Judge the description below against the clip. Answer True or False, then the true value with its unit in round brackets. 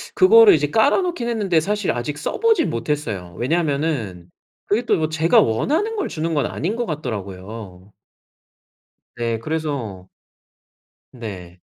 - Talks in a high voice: False (150 Hz)